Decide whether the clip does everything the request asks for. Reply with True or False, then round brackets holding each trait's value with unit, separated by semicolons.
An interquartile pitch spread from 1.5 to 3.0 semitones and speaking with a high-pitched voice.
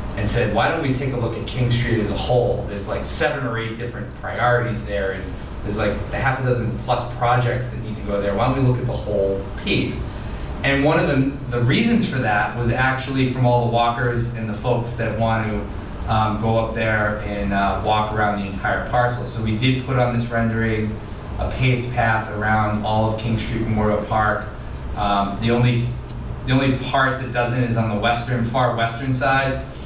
False (2.7 semitones; 115 Hz)